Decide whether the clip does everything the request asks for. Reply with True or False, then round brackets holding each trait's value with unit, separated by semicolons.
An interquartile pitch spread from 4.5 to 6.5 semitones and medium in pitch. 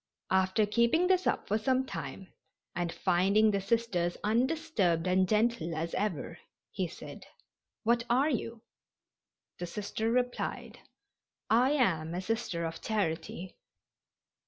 False (5.1 semitones; 210 Hz)